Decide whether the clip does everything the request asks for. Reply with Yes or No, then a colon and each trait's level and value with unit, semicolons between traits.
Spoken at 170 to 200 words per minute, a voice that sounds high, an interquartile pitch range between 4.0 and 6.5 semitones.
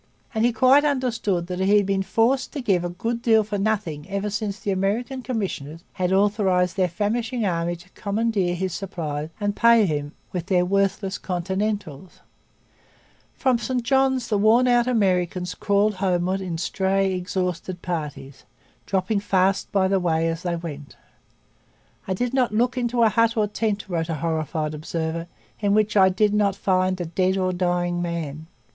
No: average, 175 wpm; high, 195 Hz; average, 3.6 semitones